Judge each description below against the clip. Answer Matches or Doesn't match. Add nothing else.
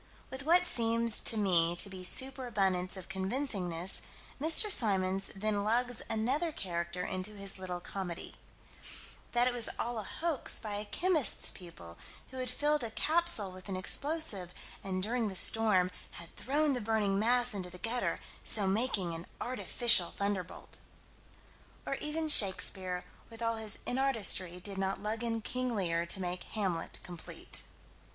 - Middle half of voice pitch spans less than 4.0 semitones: Doesn't match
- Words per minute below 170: Matches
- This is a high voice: Matches